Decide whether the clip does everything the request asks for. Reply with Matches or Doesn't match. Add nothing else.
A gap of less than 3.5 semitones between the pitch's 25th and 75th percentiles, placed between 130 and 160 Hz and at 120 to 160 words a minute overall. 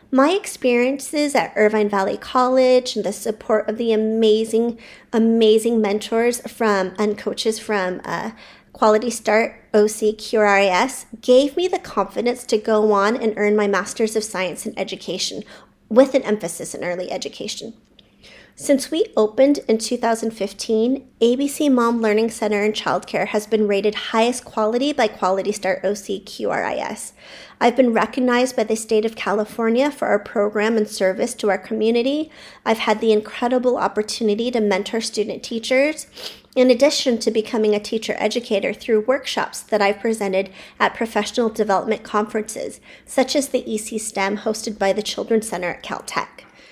Doesn't match